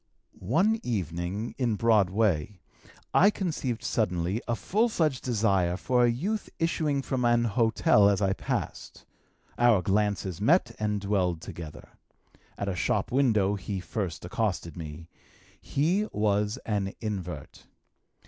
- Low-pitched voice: Yes, low, 105 Hz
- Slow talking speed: Yes, slow, 130 wpm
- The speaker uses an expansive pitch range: No, average, 4.5 semitones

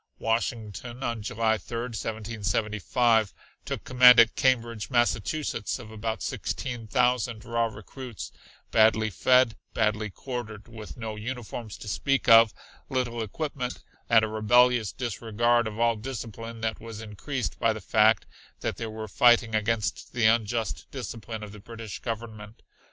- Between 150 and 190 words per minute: No, average, 140 wpm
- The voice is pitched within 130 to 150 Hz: No, low, 115 Hz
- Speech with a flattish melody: Yes, narrow, 1.8 semitones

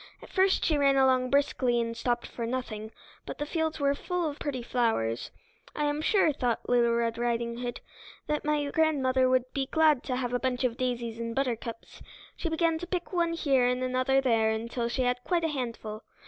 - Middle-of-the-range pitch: No, very high, 255 Hz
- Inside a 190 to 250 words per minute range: Yes, average, 200 wpm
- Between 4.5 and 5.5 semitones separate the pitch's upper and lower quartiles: No, average, 3.7 semitones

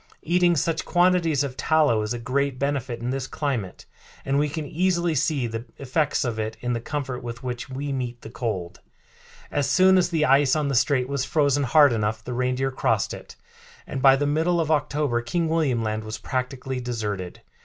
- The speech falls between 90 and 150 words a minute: No, average, 195 wpm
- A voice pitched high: No, low, 135 Hz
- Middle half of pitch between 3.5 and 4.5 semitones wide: Yes, average, 3.9 semitones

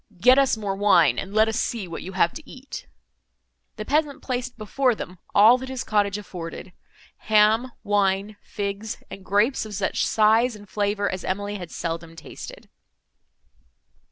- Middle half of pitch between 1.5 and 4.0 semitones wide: Yes, average, 3.0 semitones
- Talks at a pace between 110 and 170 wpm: Yes, average, 155 wpm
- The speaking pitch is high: Yes, high, 210 Hz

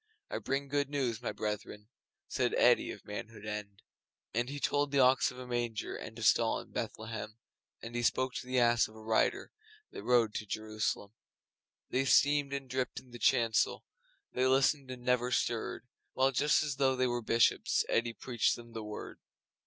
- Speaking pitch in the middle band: No, low, 120 Hz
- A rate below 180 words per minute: No, average, 185 wpm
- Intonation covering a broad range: No, average, 2.9 semitones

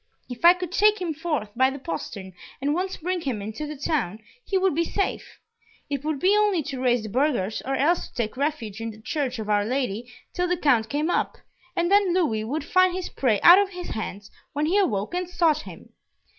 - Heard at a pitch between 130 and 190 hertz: No, very high, 290 Hz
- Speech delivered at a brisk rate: Yes, fast, 225 wpm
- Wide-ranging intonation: Yes, wide, 7.8 semitones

